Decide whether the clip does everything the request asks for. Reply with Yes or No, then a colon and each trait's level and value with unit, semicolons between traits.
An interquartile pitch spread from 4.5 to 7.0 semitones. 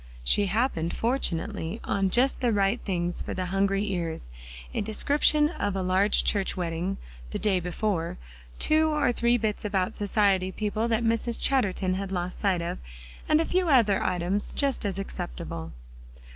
No: average, 4.1 semitones